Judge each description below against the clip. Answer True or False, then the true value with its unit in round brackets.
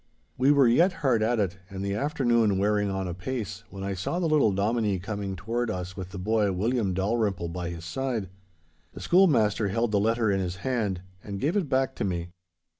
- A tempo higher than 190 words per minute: True (200 wpm)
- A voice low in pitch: True (105 Hz)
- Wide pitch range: False (4.0 semitones)